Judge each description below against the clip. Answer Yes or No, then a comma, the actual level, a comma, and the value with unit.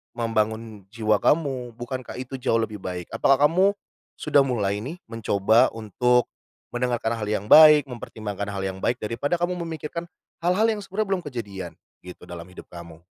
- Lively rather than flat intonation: Yes, wide, 5.7 semitones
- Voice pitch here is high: No, low, 120 Hz